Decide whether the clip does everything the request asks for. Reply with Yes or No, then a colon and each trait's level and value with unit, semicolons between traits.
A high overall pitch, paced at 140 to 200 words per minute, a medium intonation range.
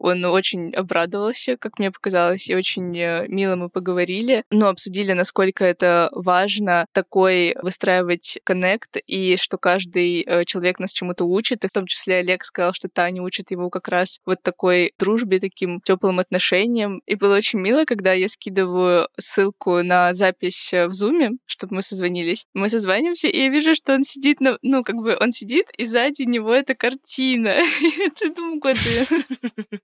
Yes: high, 195 Hz; fast, 160 wpm; average, 4.3 semitones